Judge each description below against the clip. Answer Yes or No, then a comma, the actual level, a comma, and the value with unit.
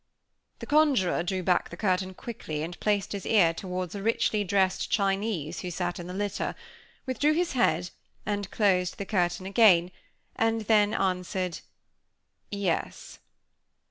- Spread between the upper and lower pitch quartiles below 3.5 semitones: Yes, average, 2.9 semitones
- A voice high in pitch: Yes, high, 195 Hz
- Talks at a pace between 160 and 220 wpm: No, average, 140 wpm